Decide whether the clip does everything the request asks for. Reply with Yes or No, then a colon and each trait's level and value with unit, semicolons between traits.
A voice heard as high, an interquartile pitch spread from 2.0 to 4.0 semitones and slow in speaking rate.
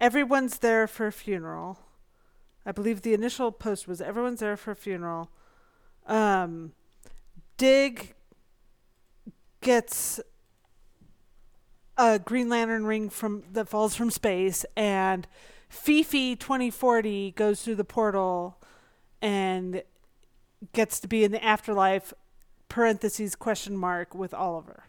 Yes: high, 215 Hz; average, 3.4 semitones; slow, 110 wpm